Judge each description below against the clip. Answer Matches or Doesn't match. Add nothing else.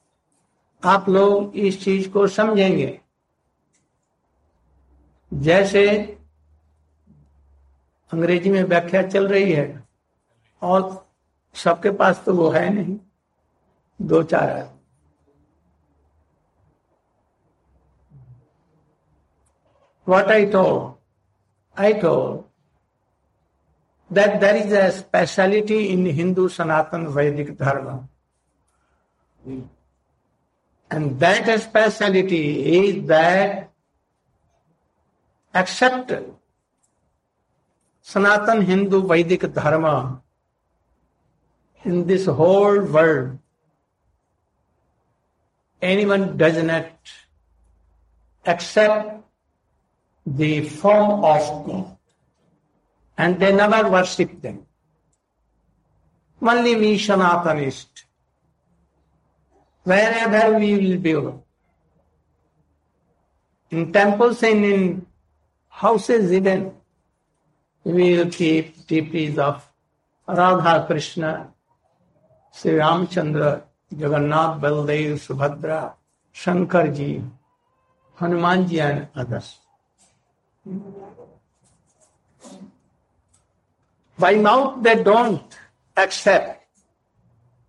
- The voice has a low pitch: Doesn't match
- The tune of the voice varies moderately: Doesn't match